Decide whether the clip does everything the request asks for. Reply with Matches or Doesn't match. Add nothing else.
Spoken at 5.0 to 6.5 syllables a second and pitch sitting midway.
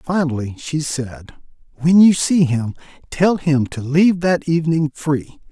Doesn't match